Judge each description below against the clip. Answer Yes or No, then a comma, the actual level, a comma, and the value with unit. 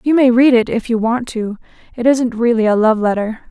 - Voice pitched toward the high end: Yes, high, 235 Hz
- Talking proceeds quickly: Yes, fast, 240 wpm